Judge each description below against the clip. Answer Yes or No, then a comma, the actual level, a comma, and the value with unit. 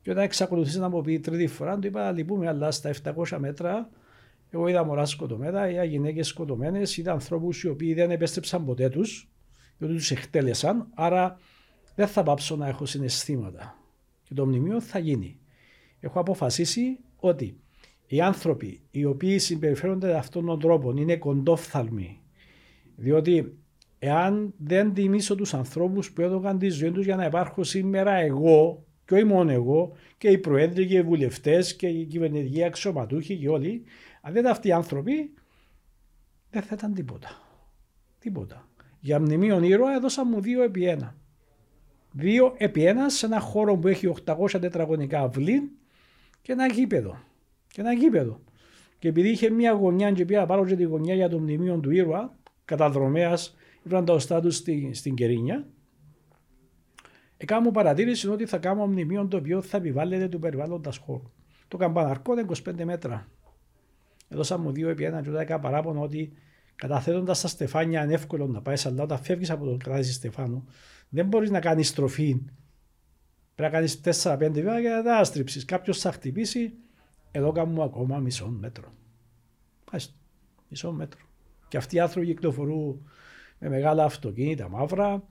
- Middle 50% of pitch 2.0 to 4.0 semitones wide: No, average, 5.0 semitones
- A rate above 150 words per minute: Yes, average, 160 wpm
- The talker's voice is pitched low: No, medium, 165 Hz